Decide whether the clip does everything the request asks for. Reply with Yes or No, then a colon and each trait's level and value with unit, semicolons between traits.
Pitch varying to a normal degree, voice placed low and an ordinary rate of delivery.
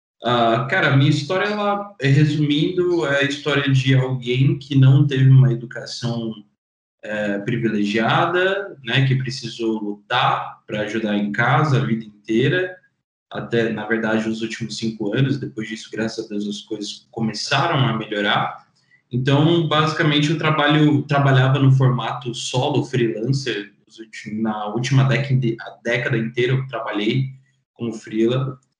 Yes: average, 4.0 semitones; low, 125 Hz; average, 135 wpm